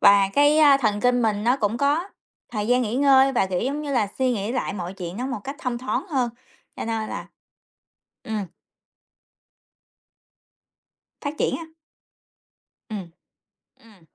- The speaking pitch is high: Yes, high, 240 Hz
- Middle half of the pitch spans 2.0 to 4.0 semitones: No, average, 4.7 semitones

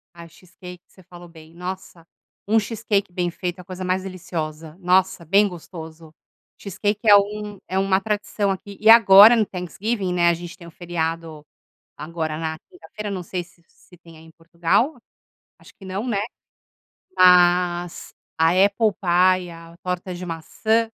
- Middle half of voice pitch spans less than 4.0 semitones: Yes, average, 2.8 semitones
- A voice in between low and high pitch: Yes, medium, 180 Hz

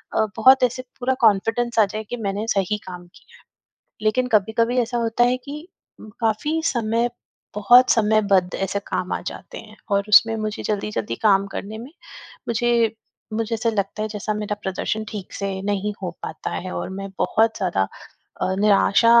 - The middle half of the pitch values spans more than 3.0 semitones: No, narrow, 2.6 semitones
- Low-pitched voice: No, high, 215 Hz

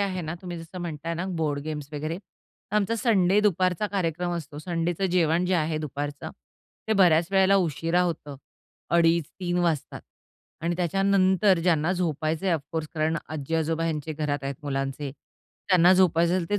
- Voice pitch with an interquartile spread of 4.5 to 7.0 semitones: No, average, 3.0 semitones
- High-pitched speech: No, medium, 165 Hz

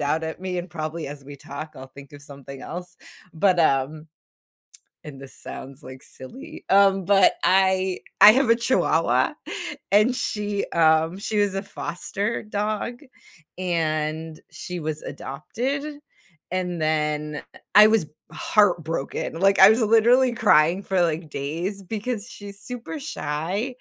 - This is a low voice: No, medium, 180 Hz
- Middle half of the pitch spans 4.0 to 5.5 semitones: Yes, average, 5.1 semitones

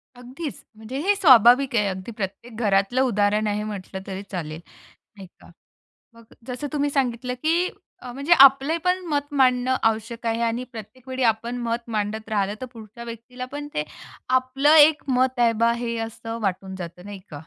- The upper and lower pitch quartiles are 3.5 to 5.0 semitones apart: Yes, average, 3.8 semitones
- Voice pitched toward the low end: No, high, 235 Hz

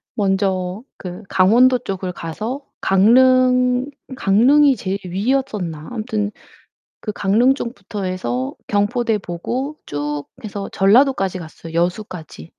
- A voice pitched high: Yes, high, 205 Hz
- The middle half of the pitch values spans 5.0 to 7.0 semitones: Yes, wide, 5.4 semitones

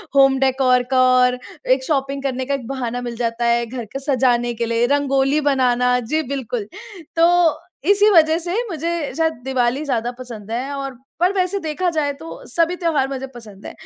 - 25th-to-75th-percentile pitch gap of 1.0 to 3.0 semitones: No, average, 3.8 semitones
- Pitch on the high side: Yes, very high, 270 Hz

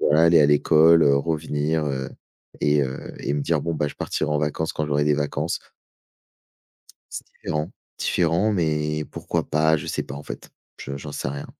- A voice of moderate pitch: No, very low, 75 Hz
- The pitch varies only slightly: Yes, narrow, 1.6 semitones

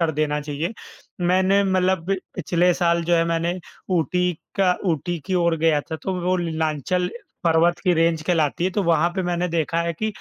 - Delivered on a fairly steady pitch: Yes, narrow, 1.8 semitones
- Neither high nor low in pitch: Yes, medium, 170 Hz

